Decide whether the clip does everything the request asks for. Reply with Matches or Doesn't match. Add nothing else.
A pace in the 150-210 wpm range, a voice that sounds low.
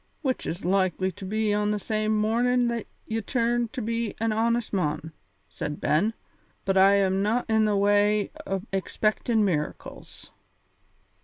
Doesn't match